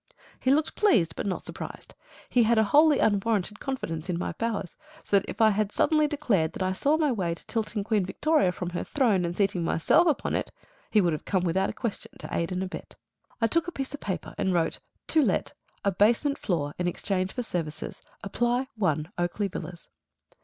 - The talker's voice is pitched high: Yes, high, 200 Hz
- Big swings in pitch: Yes, wide, 5.7 semitones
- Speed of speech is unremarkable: No, fast, 210 wpm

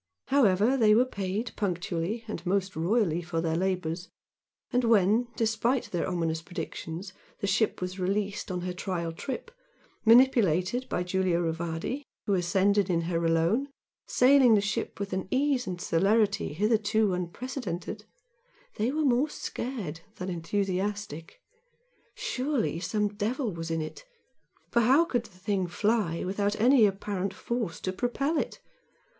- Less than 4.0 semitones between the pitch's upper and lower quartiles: No, average, 4.7 semitones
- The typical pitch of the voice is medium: No, high, 200 Hz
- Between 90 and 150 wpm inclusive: Yes, average, 140 wpm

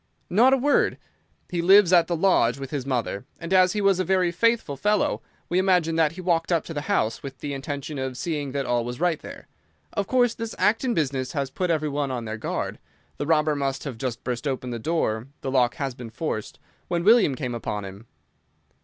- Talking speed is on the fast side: Yes, fast, 215 wpm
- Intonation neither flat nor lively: No, wide, 5.8 semitones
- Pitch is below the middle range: No, medium, 150 Hz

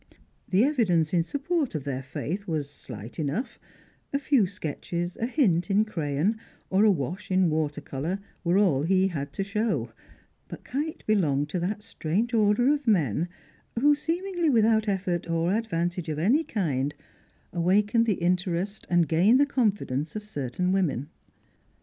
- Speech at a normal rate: Yes, average, 155 wpm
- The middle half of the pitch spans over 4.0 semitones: Yes, wide, 5.5 semitones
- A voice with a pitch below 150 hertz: No, medium, 185 Hz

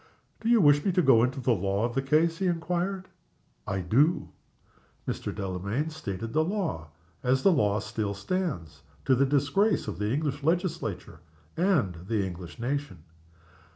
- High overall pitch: No, low, 135 Hz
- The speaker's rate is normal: Yes, average, 160 wpm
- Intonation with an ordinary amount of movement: No, wide, 8.5 semitones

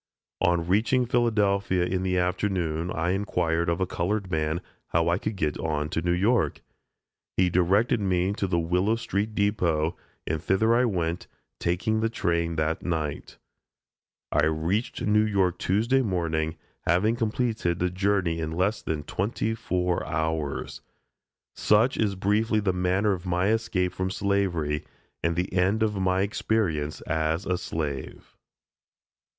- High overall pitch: No, very low, 90 Hz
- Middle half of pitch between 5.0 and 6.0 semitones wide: No, average, 3.7 semitones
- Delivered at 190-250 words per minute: No, average, 145 wpm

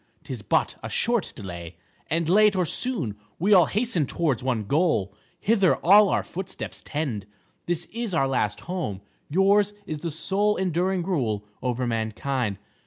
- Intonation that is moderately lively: No, wide, 7.8 semitones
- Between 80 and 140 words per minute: No, average, 155 wpm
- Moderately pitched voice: Yes, medium, 165 Hz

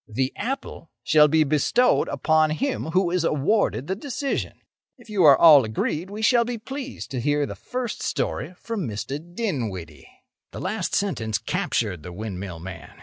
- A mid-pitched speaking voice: Yes, medium, 155 Hz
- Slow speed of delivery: No, average, 165 wpm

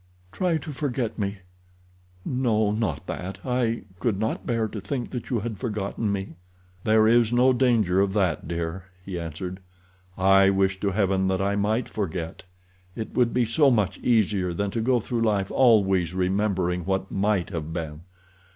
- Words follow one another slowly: No, average, 160 wpm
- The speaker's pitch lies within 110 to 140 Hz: No, low, 100 Hz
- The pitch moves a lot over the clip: No, average, 3.8 semitones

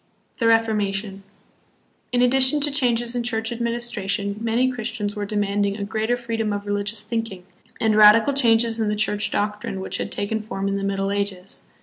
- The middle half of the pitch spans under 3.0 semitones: Yes, narrow, 2.5 semitones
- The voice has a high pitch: Yes, high, 215 Hz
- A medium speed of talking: Yes, average, 170 wpm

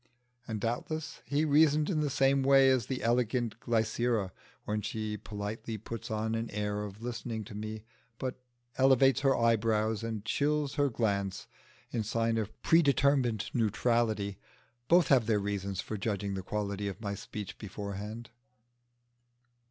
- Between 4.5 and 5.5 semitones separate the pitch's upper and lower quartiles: No, average, 3.9 semitones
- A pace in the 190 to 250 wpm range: No, average, 145 wpm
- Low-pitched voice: Yes, low, 115 Hz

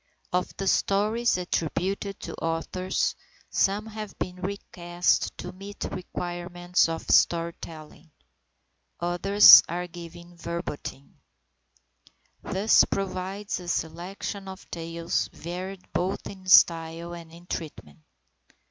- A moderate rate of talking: No, slow, 105 wpm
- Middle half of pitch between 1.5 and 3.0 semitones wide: Yes, narrow, 2.4 semitones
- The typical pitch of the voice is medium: Yes, medium, 180 Hz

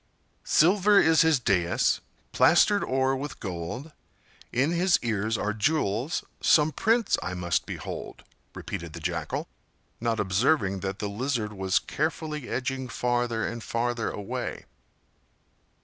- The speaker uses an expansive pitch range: Yes, wide, 7.1 semitones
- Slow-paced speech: Yes, slow, 120 wpm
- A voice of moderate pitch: No, low, 120 Hz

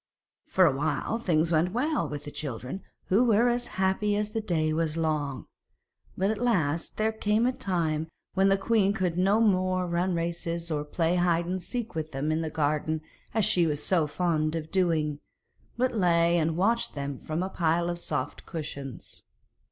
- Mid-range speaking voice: Yes, medium, 170 Hz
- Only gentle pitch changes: No, average, 3.9 semitones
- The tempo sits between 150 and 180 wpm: No, average, 190 wpm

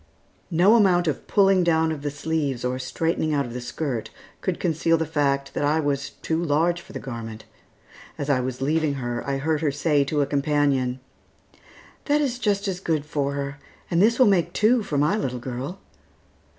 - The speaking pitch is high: No, medium, 150 Hz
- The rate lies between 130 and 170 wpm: No, average, 195 wpm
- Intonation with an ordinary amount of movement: Yes, average, 3.8 semitones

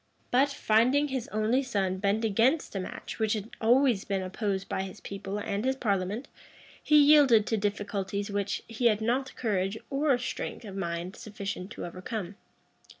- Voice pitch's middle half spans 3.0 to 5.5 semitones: Yes, average, 4.0 semitones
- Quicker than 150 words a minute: Yes, average, 165 wpm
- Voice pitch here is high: Yes, high, 215 Hz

